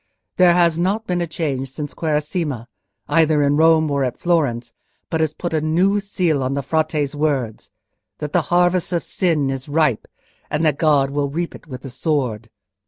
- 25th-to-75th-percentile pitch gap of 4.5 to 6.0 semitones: No, average, 3.4 semitones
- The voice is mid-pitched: Yes, medium, 155 Hz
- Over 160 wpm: Yes, average, 185 wpm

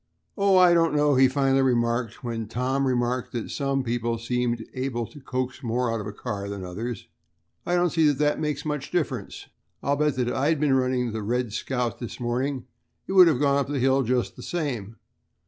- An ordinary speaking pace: No, fast, 215 wpm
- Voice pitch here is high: No, low, 130 Hz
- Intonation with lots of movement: No, average, 3.2 semitones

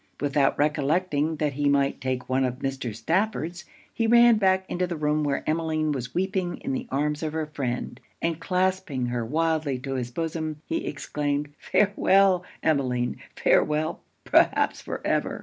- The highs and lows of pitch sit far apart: No, average, 4.3 semitones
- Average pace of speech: Yes, average, 160 wpm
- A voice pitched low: No, medium, 150 Hz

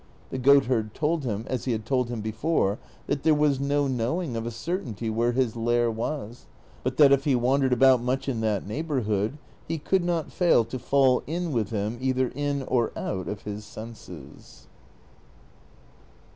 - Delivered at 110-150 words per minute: No, average, 175 wpm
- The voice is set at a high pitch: No, low, 125 Hz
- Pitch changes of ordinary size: Yes, average, 3.9 semitones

